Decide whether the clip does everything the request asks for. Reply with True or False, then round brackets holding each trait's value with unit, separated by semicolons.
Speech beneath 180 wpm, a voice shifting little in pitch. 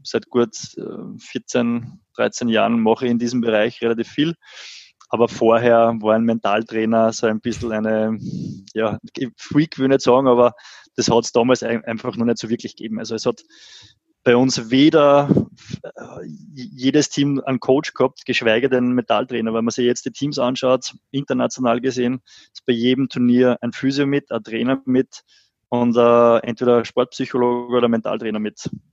True (170 wpm; 2.2 semitones)